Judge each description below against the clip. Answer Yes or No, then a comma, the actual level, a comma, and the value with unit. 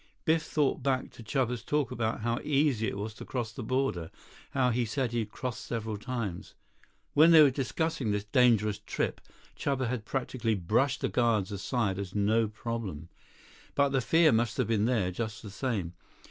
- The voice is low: Yes, low, 115 Hz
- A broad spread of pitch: No, average, 3.7 semitones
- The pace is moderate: Yes, average, 180 wpm